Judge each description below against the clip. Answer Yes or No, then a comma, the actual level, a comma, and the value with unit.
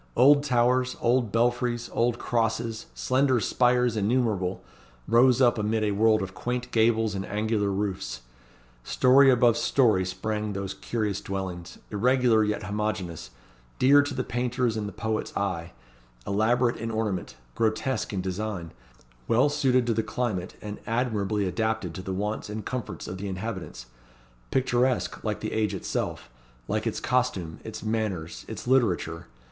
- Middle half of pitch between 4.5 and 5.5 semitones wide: No, average, 3.6 semitones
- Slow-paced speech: No, average, 145 wpm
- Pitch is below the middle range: Yes, low, 110 Hz